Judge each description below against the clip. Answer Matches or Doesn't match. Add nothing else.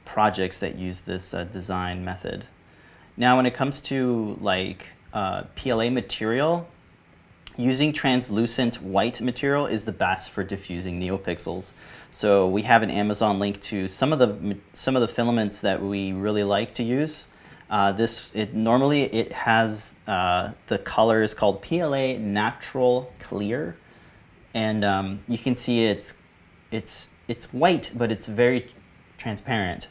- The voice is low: Matches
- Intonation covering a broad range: Doesn't match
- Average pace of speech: Matches